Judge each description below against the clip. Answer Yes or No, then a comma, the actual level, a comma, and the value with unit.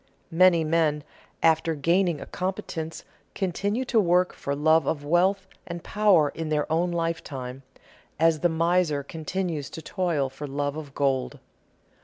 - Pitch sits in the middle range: Yes, medium, 165 Hz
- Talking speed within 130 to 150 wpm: Yes, average, 145 wpm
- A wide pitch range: No, average, 3.3 semitones